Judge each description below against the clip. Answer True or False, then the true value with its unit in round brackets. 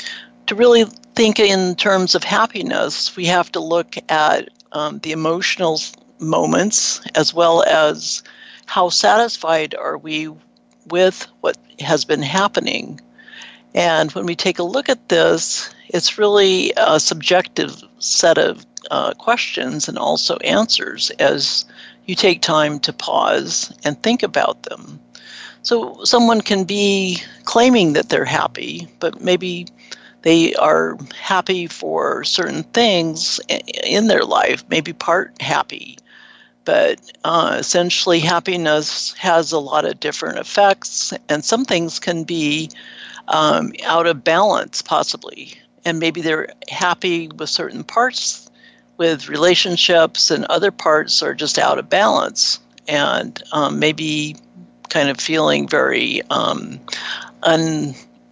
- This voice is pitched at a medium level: True (170 Hz)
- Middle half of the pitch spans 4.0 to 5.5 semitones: False (3.6 semitones)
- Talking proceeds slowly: True (130 wpm)